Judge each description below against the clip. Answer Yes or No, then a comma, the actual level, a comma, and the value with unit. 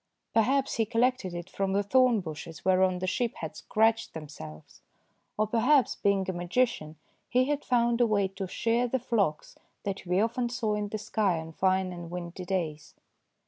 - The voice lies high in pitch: Yes, high, 200 Hz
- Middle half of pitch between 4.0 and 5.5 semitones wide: Yes, average, 4.7 semitones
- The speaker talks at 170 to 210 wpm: Yes, average, 180 wpm